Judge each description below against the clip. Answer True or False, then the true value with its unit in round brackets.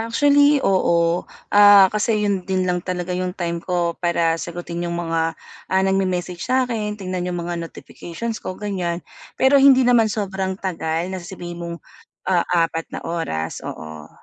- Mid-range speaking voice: True (180 Hz)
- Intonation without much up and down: False (3.1 semitones)